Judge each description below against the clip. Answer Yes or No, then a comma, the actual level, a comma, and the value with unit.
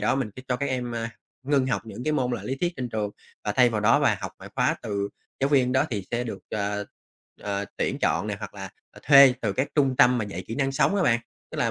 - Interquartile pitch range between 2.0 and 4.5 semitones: Yes, average, 4.0 semitones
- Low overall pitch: Yes, low, 125 Hz